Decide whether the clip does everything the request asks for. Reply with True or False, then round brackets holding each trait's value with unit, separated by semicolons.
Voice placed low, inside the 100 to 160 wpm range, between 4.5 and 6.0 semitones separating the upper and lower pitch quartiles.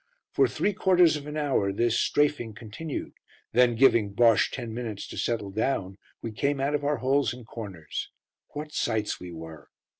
False (120 Hz; 175 wpm; 5.5 semitones)